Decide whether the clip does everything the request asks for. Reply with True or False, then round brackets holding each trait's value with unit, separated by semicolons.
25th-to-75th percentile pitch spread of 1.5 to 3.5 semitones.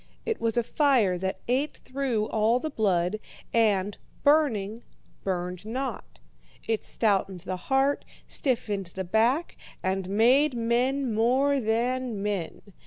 False (4.9 semitones)